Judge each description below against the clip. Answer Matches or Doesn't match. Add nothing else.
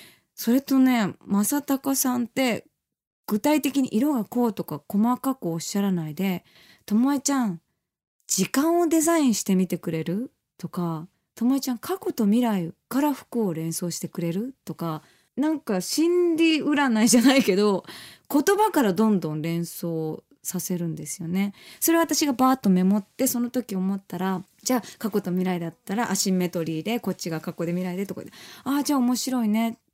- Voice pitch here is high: Matches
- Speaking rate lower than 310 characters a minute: Doesn't match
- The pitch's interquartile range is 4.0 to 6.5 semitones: Doesn't match